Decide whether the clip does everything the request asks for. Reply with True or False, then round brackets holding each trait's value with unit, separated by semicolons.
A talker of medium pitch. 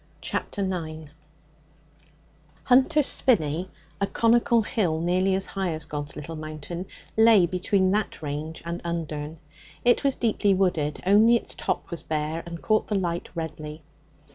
True (175 Hz)